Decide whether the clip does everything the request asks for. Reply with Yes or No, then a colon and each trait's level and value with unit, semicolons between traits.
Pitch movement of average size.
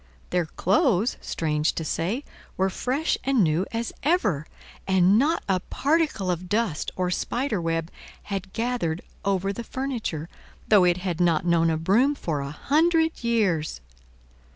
No: wide, 6.6 semitones